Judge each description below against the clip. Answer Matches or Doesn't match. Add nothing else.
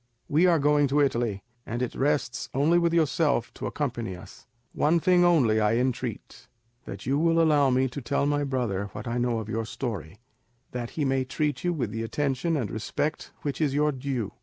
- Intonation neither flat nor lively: Matches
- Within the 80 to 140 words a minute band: Doesn't match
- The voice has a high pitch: Doesn't match